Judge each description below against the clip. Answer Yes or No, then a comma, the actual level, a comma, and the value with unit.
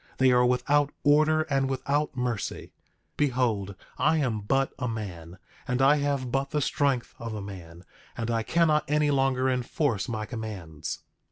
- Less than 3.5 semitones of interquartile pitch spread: No, average, 4.6 semitones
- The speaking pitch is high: No, low, 125 Hz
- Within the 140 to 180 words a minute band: Yes, average, 160 wpm